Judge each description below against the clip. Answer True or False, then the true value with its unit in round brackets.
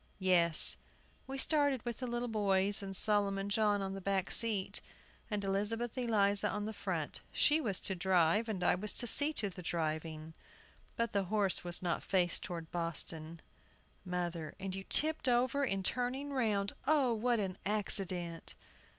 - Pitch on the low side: False (200 Hz)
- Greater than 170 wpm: False (165 wpm)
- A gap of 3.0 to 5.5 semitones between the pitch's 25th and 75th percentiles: True (4.3 semitones)